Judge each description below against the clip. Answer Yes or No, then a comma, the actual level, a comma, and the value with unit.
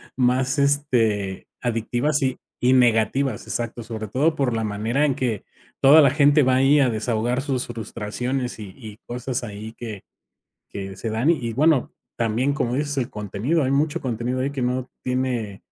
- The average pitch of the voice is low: Yes, low, 125 Hz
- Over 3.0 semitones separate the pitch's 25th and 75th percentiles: Yes, average, 3.5 semitones